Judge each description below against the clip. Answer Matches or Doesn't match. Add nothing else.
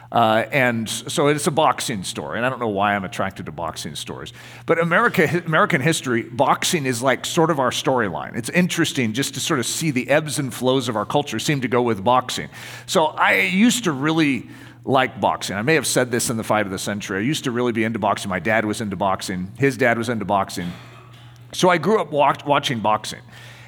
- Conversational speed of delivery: Doesn't match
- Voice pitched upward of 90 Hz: Matches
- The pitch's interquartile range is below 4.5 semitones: Doesn't match